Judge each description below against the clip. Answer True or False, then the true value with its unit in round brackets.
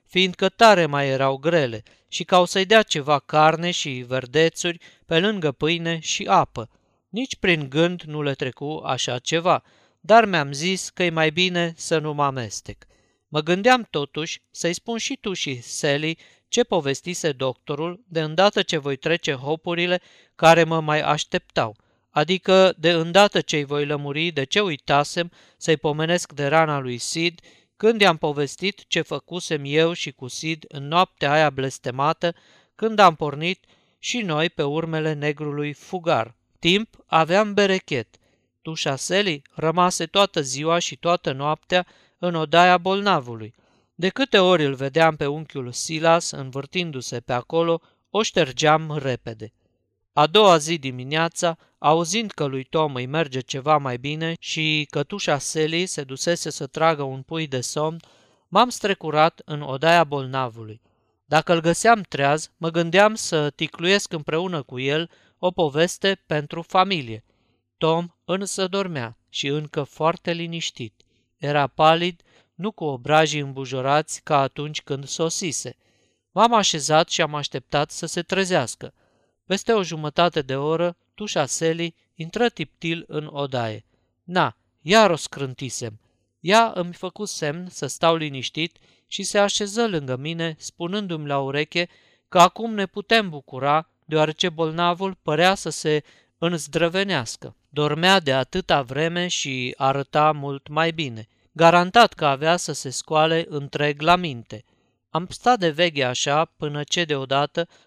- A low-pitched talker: False (160 Hz)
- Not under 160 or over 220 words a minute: False (145 wpm)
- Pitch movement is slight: False (3.7 semitones)